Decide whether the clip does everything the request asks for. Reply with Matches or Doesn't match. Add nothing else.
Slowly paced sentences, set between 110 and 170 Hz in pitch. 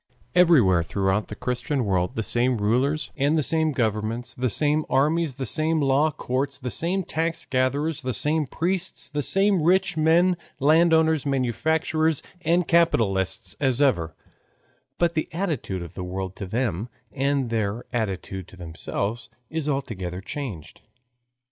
Doesn't match